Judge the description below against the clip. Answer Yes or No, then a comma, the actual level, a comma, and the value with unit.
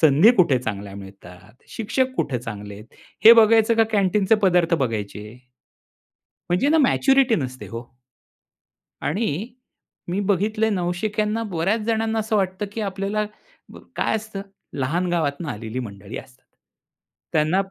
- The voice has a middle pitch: Yes, medium, 180 Hz